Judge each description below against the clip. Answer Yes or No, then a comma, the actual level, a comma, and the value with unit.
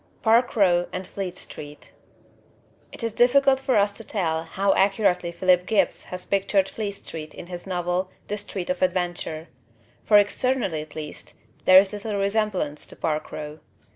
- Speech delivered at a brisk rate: No, average, 165 wpm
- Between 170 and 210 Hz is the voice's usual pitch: Yes, high, 190 Hz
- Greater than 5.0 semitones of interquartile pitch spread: No, average, 3.1 semitones